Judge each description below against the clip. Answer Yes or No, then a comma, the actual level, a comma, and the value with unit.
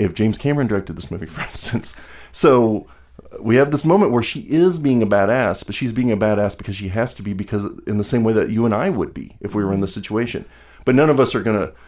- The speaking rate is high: Yes, fast, 270 wpm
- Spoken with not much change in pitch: No, average, 3.3 semitones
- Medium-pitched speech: No, low, 110 Hz